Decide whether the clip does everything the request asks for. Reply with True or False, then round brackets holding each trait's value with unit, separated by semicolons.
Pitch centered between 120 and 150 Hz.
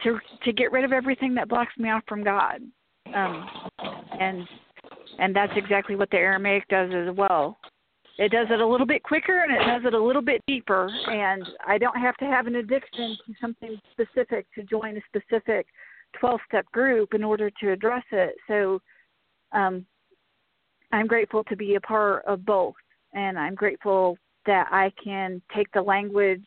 False (215 Hz)